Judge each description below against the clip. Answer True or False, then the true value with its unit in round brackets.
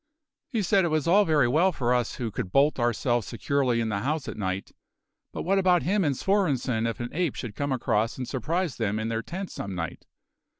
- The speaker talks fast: True (220 wpm)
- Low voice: True (130 Hz)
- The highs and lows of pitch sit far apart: True (6.9 semitones)